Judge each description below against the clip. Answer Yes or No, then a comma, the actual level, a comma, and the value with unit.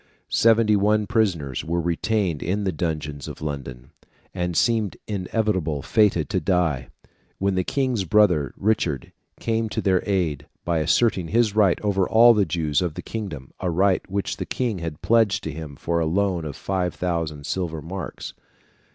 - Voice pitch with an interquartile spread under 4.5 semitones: No, average, 4.9 semitones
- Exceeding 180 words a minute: No, average, 165 wpm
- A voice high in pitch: No, very low, 90 Hz